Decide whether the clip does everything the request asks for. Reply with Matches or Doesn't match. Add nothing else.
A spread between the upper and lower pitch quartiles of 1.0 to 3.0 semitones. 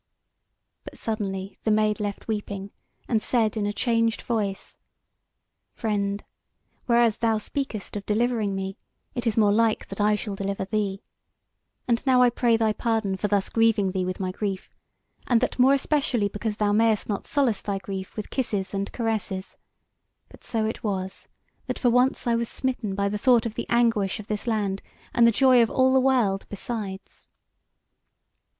Matches